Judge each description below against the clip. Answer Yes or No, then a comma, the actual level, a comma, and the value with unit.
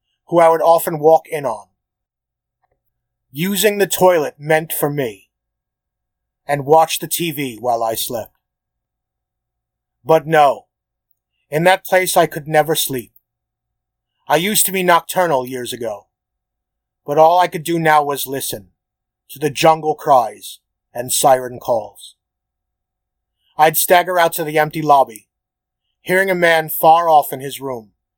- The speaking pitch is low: No, medium, 155 Hz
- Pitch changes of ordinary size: Yes, average, 4.6 semitones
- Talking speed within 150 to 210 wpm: No, average, 140 wpm